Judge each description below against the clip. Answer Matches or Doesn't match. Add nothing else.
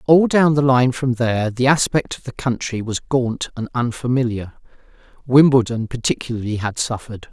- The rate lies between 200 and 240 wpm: Doesn't match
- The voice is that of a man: Matches